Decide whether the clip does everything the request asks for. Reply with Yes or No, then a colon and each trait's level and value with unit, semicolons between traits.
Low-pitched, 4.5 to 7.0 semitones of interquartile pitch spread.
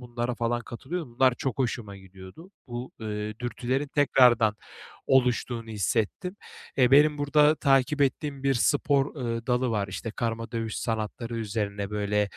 No: low, 120 Hz; average, 3.7 semitones